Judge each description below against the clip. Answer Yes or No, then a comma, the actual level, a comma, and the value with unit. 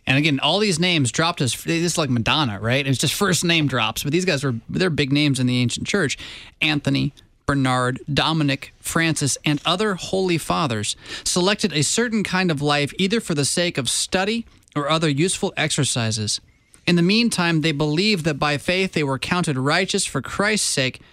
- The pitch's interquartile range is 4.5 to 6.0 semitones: Yes, average, 4.8 semitones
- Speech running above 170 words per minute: Yes, average, 190 wpm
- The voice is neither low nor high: Yes, medium, 155 Hz